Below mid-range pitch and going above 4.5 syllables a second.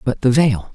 Yes: low, 130 Hz; 4.8 syllables/s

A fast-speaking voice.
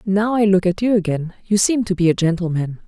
Yes: fast, 250 wpm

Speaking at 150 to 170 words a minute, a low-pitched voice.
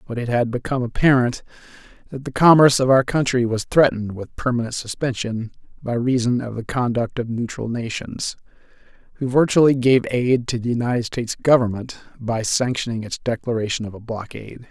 Yes: average, 165 wpm; low, 120 Hz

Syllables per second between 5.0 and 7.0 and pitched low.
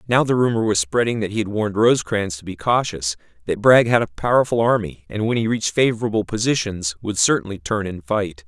Yes: 6.0 syllables/s; low, 105 Hz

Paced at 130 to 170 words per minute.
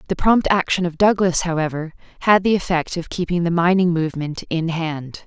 No: average, 180 wpm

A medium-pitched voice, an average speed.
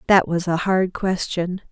Yes: medium, 180 Hz; average, 175 wpm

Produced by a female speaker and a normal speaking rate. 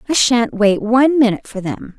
No: female; fast, 210 wpm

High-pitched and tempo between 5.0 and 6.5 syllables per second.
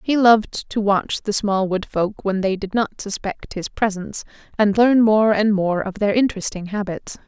No: high, 205 Hz; 4.8 syllables/s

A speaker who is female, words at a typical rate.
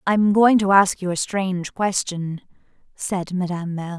Yes: female; average, 165 wpm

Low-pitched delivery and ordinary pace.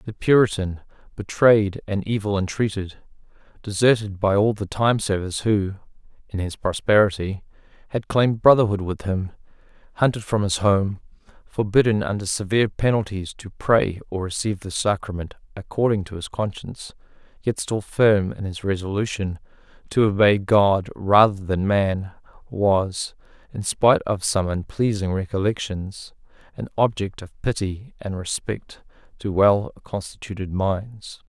No: low, 100 Hz; slow, 130 wpm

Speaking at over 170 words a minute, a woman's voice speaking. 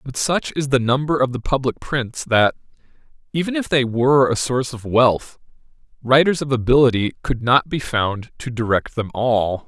No: average, 180 wpm; male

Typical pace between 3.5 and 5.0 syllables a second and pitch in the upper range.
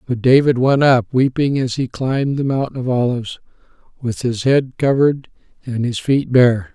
No: 4.8 syllables/s; low, 130 Hz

